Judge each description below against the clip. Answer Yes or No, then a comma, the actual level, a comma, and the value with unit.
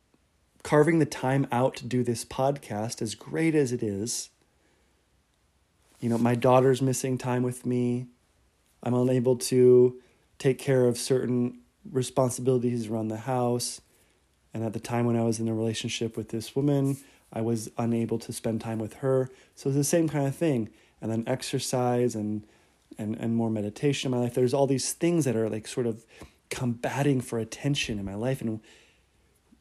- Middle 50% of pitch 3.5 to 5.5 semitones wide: No, narrow, 2.6 semitones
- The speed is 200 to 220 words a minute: No, average, 175 wpm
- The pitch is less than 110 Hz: No, low, 125 Hz